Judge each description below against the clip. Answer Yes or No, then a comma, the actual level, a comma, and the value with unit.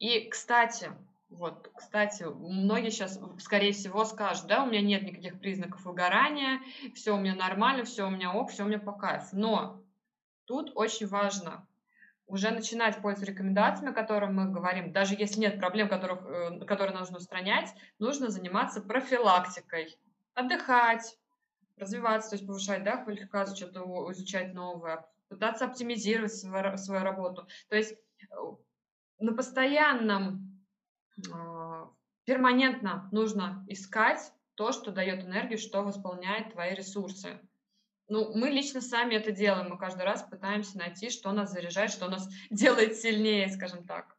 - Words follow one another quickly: No, average, 140 wpm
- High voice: Yes, high, 205 Hz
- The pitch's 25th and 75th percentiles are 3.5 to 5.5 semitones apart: No, average, 2.8 semitones